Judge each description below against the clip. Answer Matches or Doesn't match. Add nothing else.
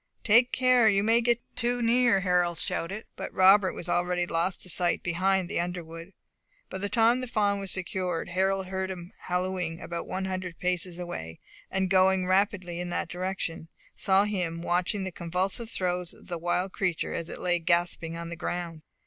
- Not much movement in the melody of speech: Matches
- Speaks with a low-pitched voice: Doesn't match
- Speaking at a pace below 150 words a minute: Doesn't match